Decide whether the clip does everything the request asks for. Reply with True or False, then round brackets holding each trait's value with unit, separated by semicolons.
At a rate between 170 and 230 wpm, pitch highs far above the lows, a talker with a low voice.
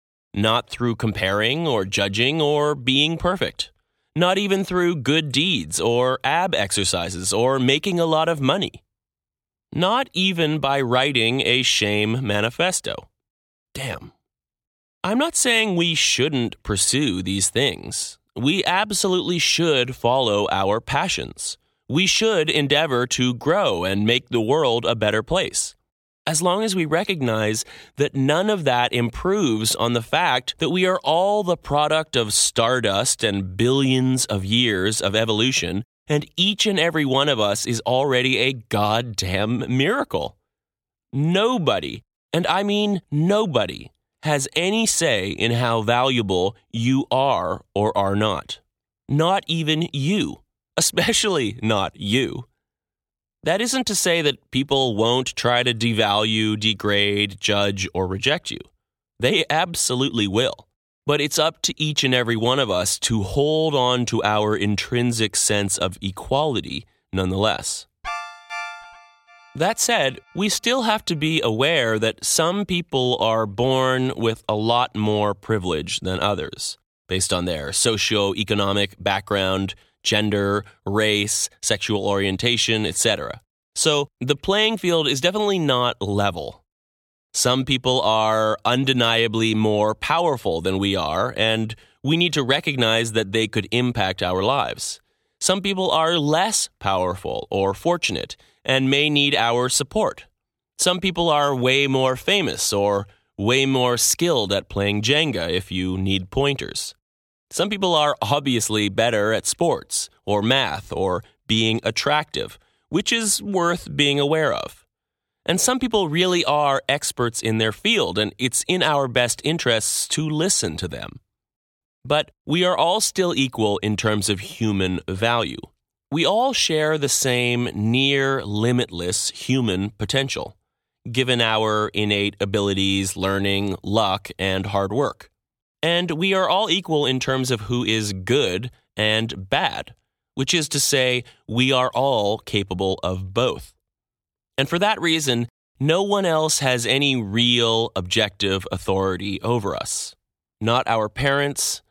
False (135 wpm; 6.4 semitones; 125 Hz)